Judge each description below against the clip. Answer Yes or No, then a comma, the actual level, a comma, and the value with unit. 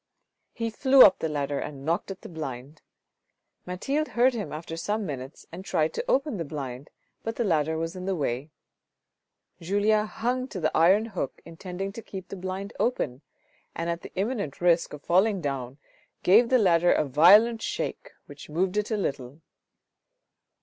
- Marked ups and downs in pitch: Yes, wide, 5.7 semitones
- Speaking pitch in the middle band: Yes, medium, 180 Hz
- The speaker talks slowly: No, average, 175 wpm